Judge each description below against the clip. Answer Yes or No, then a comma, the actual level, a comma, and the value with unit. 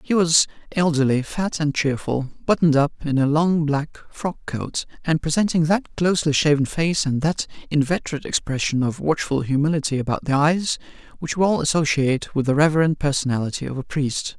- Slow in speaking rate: No, average, 165 wpm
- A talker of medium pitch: Yes, medium, 150 Hz